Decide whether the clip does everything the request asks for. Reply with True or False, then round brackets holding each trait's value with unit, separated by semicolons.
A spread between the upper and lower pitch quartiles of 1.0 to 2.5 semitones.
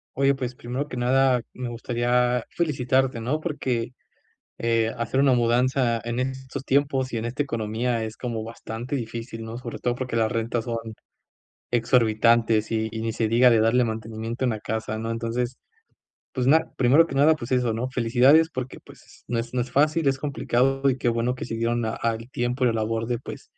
True (2.2 semitones)